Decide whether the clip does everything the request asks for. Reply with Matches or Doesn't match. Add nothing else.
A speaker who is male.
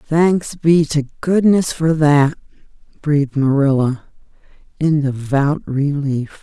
Doesn't match